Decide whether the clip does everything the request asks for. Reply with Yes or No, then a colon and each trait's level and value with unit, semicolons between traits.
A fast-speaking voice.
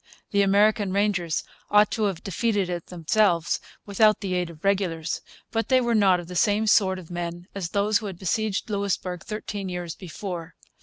No: average, 175 wpm